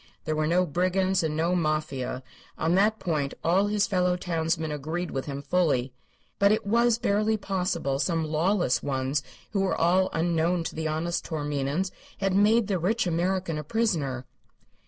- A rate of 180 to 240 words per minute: No, average, 165 wpm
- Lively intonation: No, average, 3.9 semitones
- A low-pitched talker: No, medium, 170 Hz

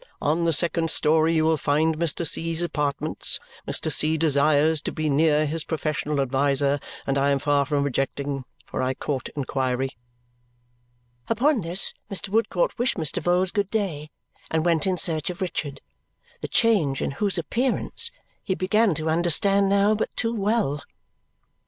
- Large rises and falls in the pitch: No, average, 4.7 semitones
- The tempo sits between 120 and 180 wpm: Yes, average, 160 wpm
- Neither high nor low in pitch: Yes, medium, 160 Hz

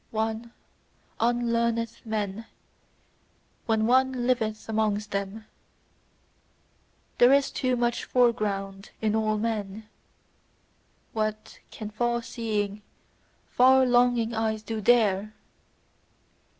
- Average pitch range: No, narrow, 1.9 semitones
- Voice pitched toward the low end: No, high, 225 Hz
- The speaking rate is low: Yes, slow, 90 wpm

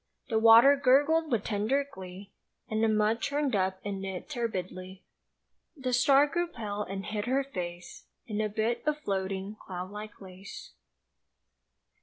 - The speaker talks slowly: No, average, 150 wpm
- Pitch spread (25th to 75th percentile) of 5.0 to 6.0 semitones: Yes, wide, 5.4 semitones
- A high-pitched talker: Yes, high, 215 Hz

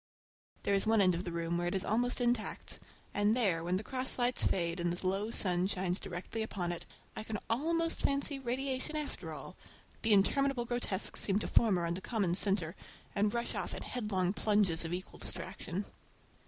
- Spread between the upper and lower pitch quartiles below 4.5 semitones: No, average, 5.1 semitones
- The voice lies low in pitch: No, high, 205 Hz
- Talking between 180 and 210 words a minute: Yes, average, 190 wpm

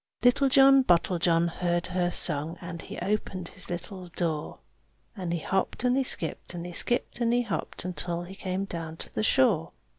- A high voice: No, medium, 180 Hz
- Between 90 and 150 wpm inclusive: No, average, 185 wpm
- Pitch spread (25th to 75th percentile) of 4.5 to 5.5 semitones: No, average, 4.1 semitones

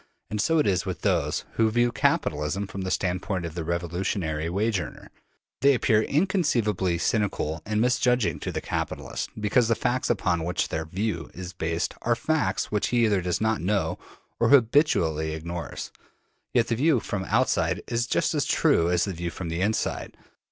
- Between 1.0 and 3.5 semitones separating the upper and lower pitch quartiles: No, average, 5.3 semitones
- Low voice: Yes, low, 100 Hz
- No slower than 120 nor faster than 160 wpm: No, average, 185 wpm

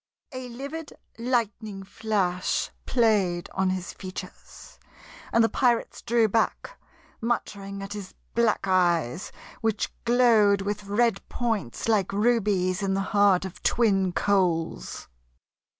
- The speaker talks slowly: Yes, slow, 120 wpm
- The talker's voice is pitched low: No, high, 205 Hz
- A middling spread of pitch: Yes, average, 3.3 semitones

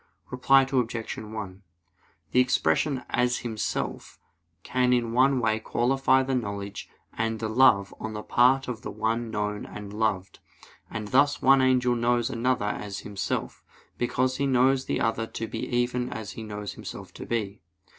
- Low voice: Yes, low, 120 Hz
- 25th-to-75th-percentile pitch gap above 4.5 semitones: No, average, 3.1 semitones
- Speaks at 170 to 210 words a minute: No, average, 160 wpm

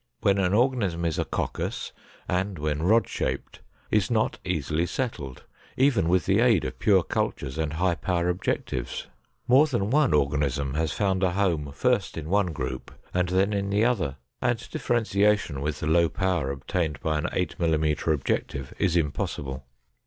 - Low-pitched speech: Yes, very low, 90 Hz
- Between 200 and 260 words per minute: No, average, 165 wpm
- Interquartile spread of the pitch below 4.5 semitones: No, average, 5.2 semitones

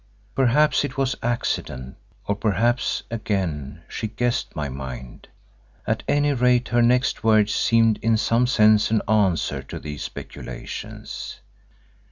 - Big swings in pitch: Yes, wide, 5.8 semitones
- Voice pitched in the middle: No, low, 110 Hz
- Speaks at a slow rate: Yes, slow, 130 wpm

